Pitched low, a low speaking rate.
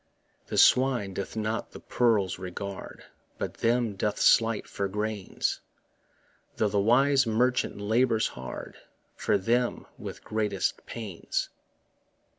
Yes: low, 110 Hz; slow, 115 wpm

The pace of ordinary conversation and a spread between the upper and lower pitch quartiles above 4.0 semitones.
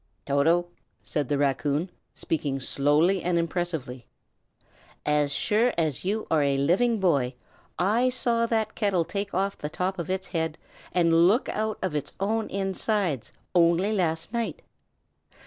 Yes: average, 145 wpm; average, 5.2 semitones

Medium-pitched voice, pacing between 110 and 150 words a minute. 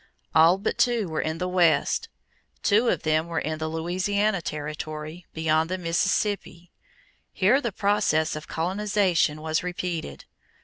Yes: medium, 170 Hz; average, 140 wpm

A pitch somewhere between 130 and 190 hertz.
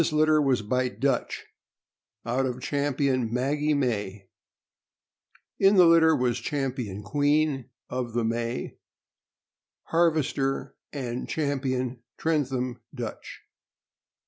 Yes: low, 135 Hz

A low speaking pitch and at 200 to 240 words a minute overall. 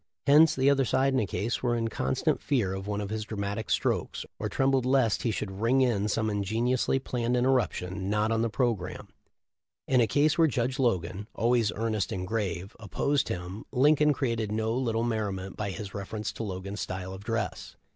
Yes: low, 110 Hz; fast, 205 wpm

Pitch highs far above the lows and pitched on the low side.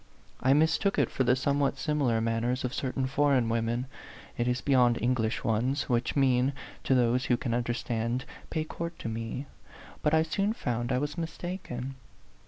No: average, 3.2 semitones; low, 130 Hz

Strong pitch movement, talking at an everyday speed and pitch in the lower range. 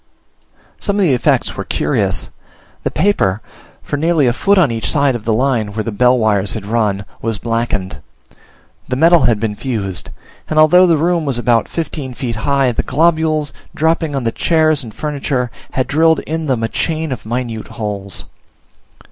Yes: wide, 5.7 semitones; average, 180 wpm; low, 130 Hz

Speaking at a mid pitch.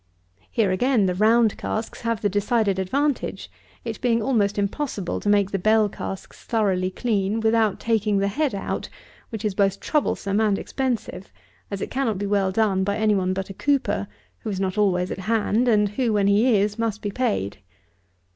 No: high, 210 Hz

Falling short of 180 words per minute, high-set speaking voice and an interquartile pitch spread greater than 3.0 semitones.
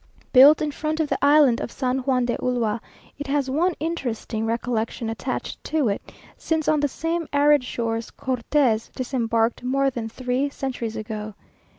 Yes: average, 165 wpm; very high, 255 Hz; average, 3.9 semitones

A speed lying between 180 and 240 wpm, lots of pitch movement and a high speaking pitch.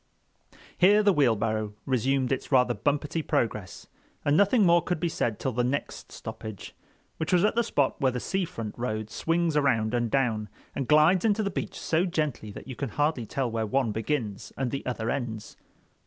No: average, 190 wpm; wide, 6.0 semitones; low, 135 Hz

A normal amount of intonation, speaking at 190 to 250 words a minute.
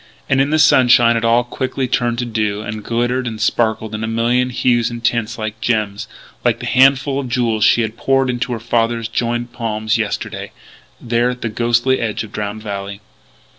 No: narrow, 2.0 semitones; average, 195 wpm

